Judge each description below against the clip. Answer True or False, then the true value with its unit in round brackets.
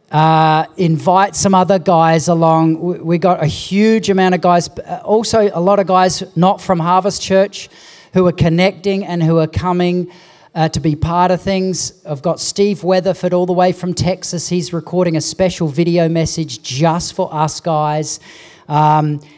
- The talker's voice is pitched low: False (175 Hz)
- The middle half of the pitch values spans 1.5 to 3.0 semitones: True (2.6 semitones)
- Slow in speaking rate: False (175 wpm)